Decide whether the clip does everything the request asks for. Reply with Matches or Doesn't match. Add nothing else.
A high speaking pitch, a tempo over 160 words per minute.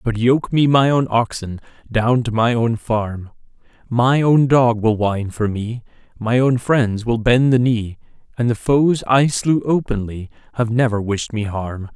Doesn't match